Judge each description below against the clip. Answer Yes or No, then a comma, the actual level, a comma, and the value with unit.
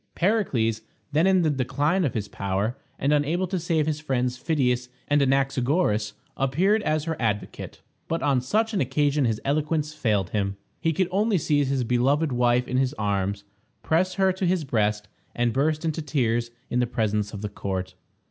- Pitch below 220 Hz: Yes, low, 135 Hz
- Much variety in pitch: Yes, wide, 5.7 semitones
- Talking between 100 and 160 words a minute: No, average, 175 wpm